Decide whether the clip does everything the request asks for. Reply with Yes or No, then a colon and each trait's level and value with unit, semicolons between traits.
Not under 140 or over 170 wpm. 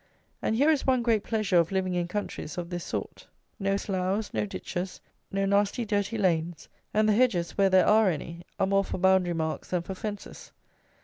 No: average, 195 wpm